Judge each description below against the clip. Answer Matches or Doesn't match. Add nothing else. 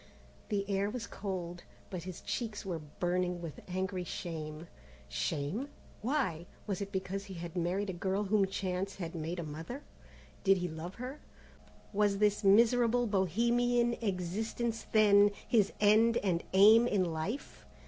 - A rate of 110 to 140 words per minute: Doesn't match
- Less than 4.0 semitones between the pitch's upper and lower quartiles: Matches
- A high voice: Matches